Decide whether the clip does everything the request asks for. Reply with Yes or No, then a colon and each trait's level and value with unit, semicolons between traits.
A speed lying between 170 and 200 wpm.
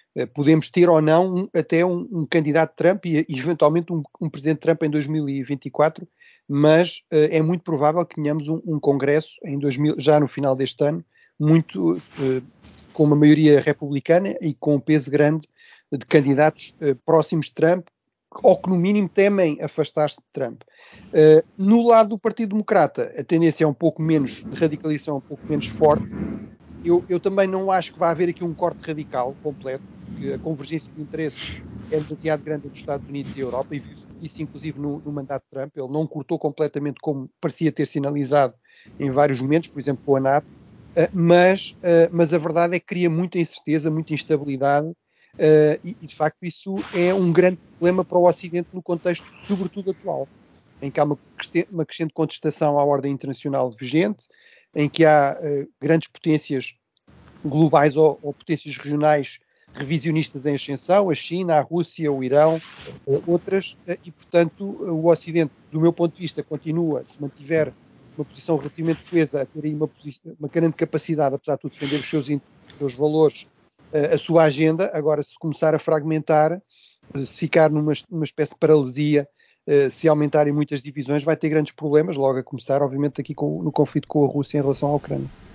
Yes: average, 180 wpm